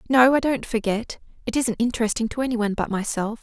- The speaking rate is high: No, average, 195 wpm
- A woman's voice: Yes, female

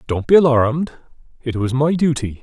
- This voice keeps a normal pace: Yes, average, 175 wpm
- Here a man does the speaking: Yes, male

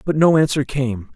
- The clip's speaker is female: No, male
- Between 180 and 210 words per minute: Yes, fast, 205 wpm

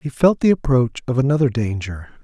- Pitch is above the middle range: No, low, 130 Hz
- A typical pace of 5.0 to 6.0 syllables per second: Yes, 5.4 syllables/s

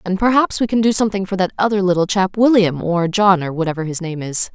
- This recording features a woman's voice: Yes, female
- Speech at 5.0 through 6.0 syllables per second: No, 6.2 syllables/s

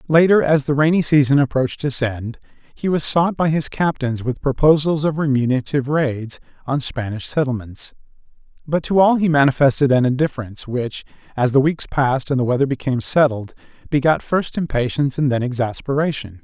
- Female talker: No, male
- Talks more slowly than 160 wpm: No, average, 165 wpm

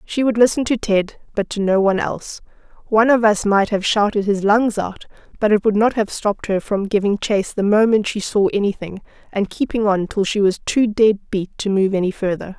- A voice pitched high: Yes, high, 205 Hz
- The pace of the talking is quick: Yes, fast, 225 wpm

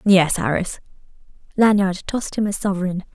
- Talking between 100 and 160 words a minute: Yes, slow, 135 wpm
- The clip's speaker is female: Yes, female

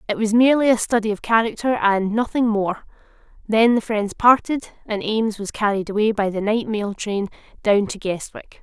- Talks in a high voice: Yes, high, 215 Hz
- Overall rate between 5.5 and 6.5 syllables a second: No, 5.1 syllables/s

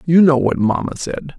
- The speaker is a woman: No, male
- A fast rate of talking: Yes, fast, 215 wpm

